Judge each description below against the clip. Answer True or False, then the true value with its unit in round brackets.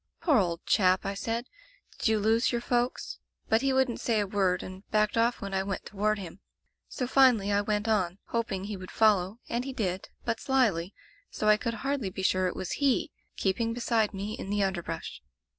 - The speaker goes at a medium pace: False (210 wpm)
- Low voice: False (210 Hz)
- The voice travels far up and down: False (3.4 semitones)